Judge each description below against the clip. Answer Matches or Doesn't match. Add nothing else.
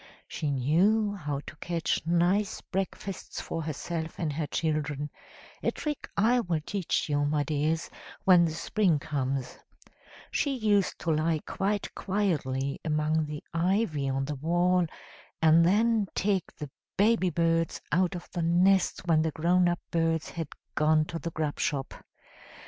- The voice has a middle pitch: Matches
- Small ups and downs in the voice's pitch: Doesn't match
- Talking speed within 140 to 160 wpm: Matches